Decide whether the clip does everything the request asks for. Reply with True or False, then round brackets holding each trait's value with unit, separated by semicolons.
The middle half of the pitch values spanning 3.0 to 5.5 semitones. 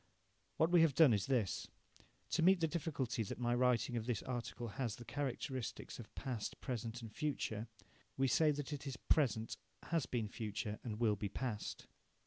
True (4.3 semitones)